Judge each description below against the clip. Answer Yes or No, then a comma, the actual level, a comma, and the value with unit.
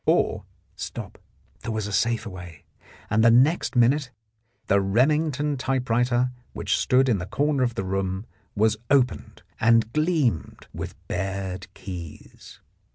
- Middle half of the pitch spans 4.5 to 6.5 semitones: Yes, average, 5.3 semitones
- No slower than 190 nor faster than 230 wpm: No, slow, 135 wpm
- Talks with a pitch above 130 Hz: No, low, 115 Hz